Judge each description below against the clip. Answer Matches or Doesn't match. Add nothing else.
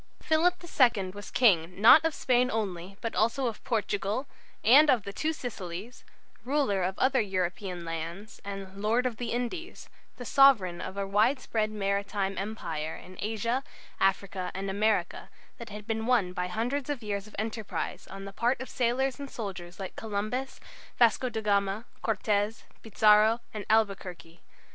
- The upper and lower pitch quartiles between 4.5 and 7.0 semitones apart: Doesn't match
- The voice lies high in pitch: Matches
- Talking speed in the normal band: Matches